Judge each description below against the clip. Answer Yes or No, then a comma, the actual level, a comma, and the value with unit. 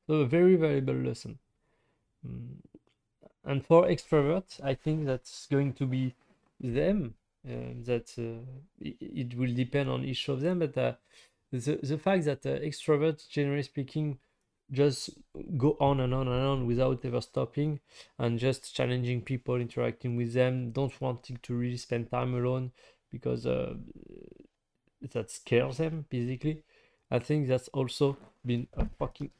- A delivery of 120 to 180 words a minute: Yes, average, 150 wpm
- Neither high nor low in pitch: No, low, 130 Hz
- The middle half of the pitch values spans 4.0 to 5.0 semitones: No, average, 3.1 semitones